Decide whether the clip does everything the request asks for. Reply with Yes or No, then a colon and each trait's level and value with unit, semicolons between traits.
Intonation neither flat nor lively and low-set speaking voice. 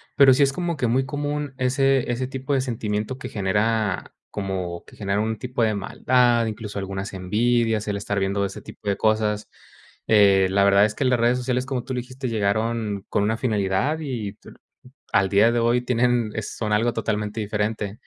Yes: average, 3.6 semitones; low, 110 Hz